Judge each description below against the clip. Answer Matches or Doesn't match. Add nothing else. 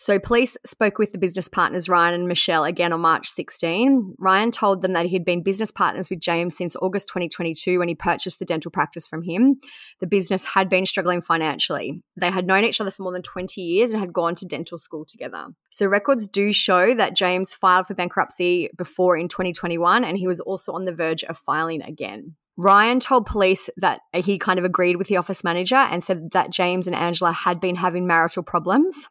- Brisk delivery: Matches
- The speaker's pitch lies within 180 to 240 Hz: Matches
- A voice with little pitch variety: Matches